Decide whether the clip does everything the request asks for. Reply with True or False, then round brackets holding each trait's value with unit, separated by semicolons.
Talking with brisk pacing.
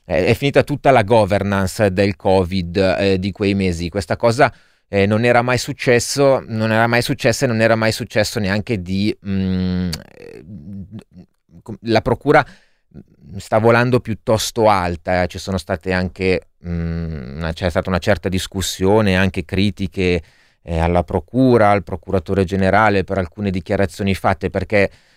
False (140 wpm)